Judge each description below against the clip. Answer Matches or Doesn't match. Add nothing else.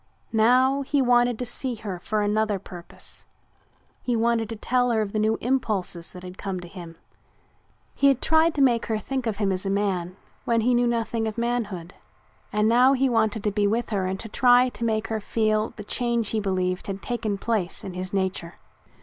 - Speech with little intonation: Doesn't match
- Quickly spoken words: Matches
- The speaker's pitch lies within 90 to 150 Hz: Doesn't match